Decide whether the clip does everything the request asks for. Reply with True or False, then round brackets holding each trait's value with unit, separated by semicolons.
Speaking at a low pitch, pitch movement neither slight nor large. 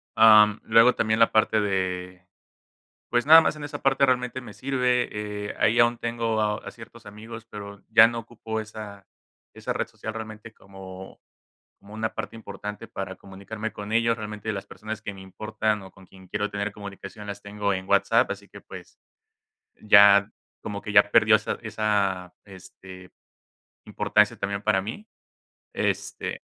False (105 Hz; 2.1 semitones)